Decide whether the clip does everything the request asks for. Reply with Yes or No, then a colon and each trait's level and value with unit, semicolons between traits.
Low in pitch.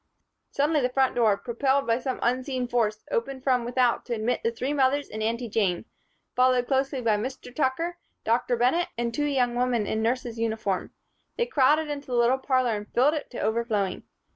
No: very high, 250 Hz